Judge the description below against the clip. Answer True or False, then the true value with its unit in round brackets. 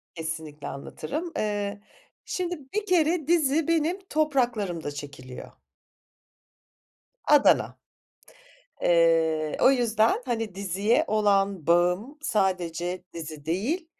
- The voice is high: True (205 Hz)